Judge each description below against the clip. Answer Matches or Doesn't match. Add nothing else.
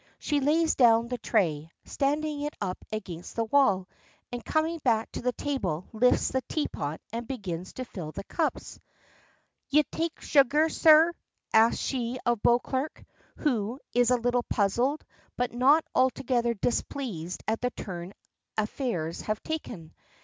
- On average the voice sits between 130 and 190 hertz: Doesn't match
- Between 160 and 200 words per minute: Doesn't match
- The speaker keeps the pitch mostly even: Doesn't match